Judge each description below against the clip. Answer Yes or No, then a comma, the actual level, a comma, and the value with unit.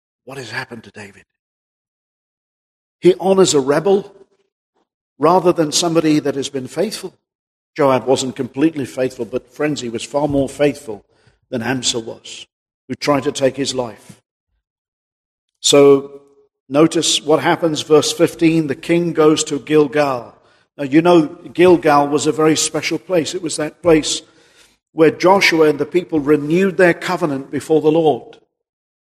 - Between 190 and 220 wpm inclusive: No, average, 145 wpm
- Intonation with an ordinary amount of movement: Yes, average, 3.5 semitones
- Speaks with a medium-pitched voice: Yes, medium, 150 Hz